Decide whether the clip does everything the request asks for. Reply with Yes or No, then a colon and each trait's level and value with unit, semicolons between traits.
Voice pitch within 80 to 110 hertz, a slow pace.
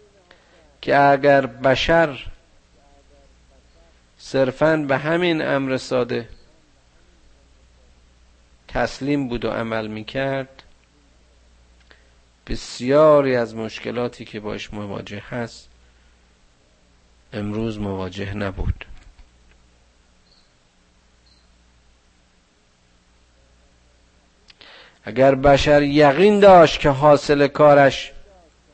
Yes: very low, 95 Hz; slow, 65 wpm